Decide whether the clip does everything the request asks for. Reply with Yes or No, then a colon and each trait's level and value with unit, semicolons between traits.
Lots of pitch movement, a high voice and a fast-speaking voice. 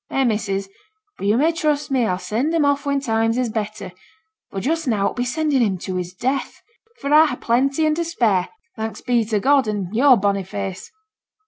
Yes: wide, 5.7 semitones; high, 235 Hz; fast, 215 wpm